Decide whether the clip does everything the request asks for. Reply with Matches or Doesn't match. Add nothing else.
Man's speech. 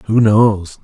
Matches